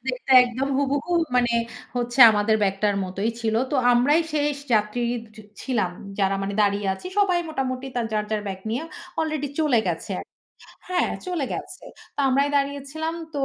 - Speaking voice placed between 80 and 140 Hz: No, very high, 250 Hz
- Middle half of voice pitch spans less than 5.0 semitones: No, wide, 5.5 semitones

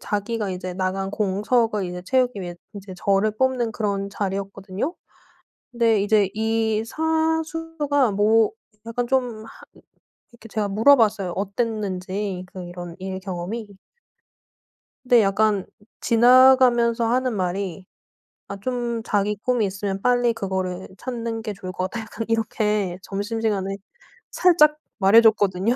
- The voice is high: Yes, high, 215 Hz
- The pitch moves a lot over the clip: No, average, 3.5 semitones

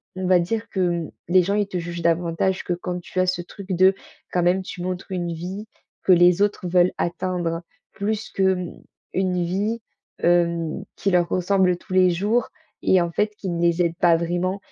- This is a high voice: No, medium, 180 Hz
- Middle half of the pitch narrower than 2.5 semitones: Yes, narrow, 1.7 semitones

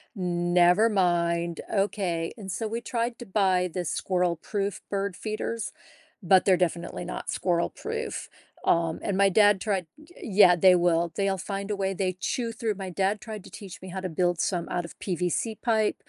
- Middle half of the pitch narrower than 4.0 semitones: Yes, average, 2.9 semitones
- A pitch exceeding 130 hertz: Yes, high, 190 Hz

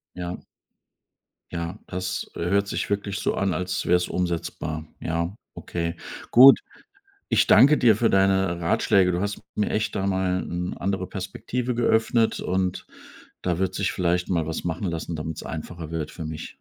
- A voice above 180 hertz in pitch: No, very low, 90 Hz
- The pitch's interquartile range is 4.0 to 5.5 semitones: No, narrow, 2.6 semitones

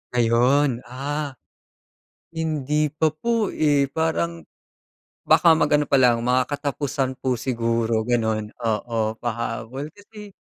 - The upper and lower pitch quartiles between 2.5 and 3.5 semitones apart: No, average, 4.3 semitones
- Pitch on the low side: Yes, low, 130 Hz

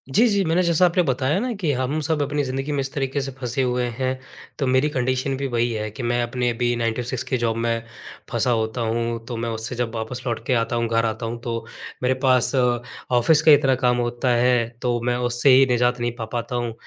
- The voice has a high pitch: No, low, 125 Hz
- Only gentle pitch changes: Yes, narrow, 2.2 semitones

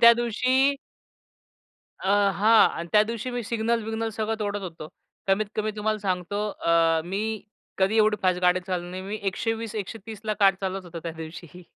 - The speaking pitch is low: No, high, 205 Hz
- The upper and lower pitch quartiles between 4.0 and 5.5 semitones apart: No, average, 3.6 semitones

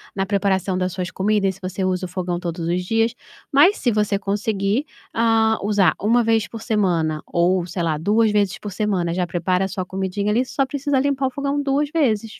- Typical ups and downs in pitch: Yes, average, 3.7 semitones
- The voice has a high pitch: Yes, high, 200 Hz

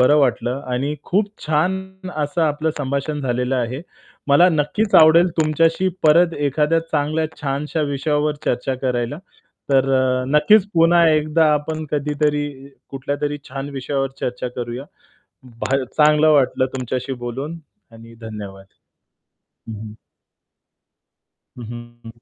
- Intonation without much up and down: No, average, 3.3 semitones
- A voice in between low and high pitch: Yes, medium, 145 Hz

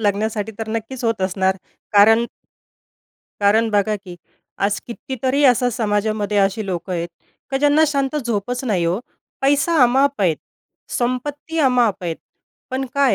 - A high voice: Yes, high, 225 Hz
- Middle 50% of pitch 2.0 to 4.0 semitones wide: No, average, 4.6 semitones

